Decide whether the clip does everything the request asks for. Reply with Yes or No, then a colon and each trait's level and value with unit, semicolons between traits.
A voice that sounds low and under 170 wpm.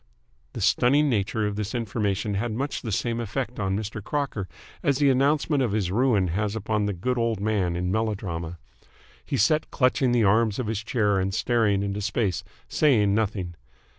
No: low, 110 Hz; average, 180 wpm